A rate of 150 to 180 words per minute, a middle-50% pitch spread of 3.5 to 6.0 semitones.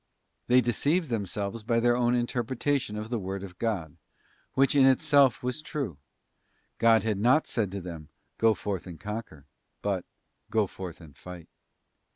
Yes: average, 160 wpm; average, 4.6 semitones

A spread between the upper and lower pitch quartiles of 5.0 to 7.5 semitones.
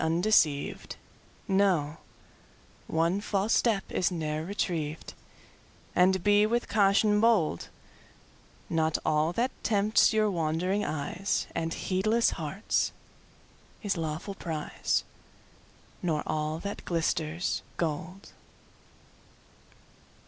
No: average, 4.4 semitones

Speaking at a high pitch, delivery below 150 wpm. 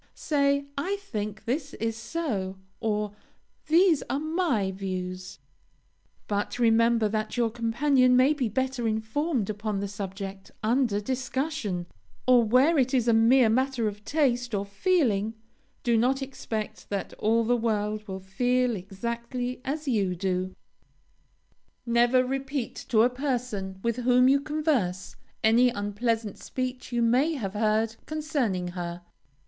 Yes: high, 235 Hz; slow, 135 wpm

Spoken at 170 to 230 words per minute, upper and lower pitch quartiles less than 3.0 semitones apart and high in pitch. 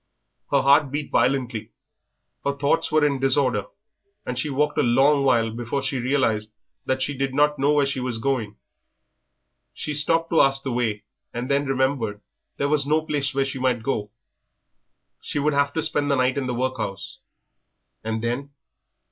No: average, 175 wpm; narrow, 2.6 semitones; low, 135 Hz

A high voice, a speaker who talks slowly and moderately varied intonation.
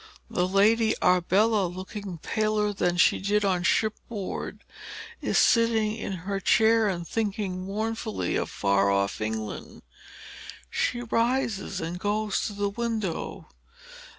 Yes: high, 205 Hz; slow, 125 wpm; average, 3.3 semitones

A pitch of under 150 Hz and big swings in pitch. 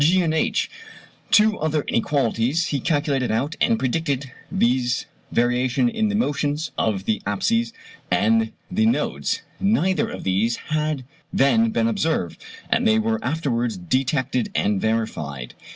Yes: low, 135 Hz; wide, 6.6 semitones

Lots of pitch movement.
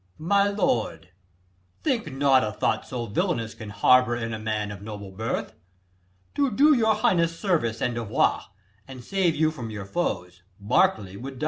Yes: wide, 8.3 semitones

